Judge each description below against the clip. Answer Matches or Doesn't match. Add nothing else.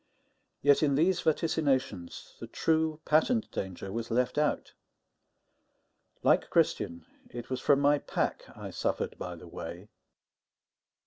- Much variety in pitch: Matches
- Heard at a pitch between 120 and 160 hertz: Matches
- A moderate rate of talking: Doesn't match